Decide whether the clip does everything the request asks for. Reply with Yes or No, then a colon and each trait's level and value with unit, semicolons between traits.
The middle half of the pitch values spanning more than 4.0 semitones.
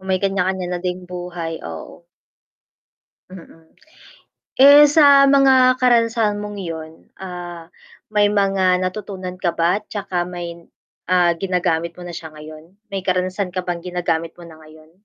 No: average, 2.9 semitones